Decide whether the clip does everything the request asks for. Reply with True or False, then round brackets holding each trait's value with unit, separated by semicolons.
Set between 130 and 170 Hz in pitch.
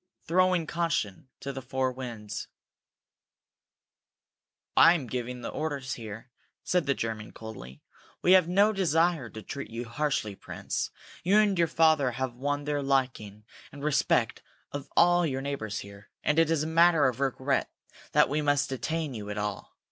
True (140 Hz)